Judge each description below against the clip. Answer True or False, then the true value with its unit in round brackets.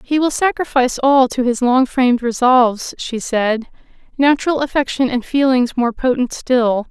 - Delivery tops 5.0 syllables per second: False (4.8 syllables/s)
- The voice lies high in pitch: True (255 Hz)